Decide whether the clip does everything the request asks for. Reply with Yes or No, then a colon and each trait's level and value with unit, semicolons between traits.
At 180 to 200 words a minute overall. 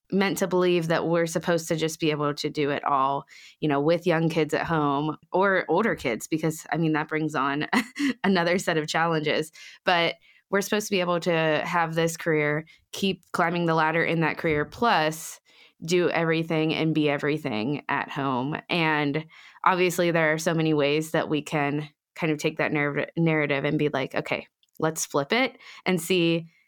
Yes: average, 190 wpm